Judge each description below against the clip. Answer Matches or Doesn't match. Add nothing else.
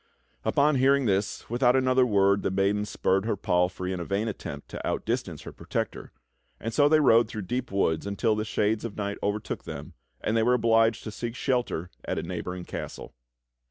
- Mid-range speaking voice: Doesn't match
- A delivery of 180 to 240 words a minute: Matches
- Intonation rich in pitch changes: Doesn't match